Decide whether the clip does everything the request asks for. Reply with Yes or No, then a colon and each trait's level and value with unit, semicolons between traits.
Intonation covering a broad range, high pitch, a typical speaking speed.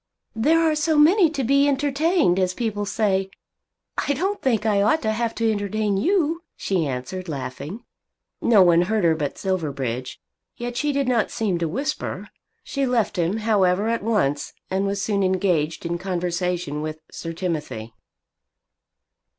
Yes: wide, 6.5 semitones; high, 200 Hz; average, 160 wpm